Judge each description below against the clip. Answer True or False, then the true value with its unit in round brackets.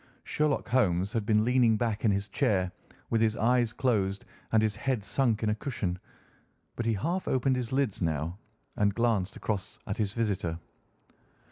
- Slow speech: False (170 wpm)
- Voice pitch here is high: False (110 Hz)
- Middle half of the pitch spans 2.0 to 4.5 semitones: True (3.4 semitones)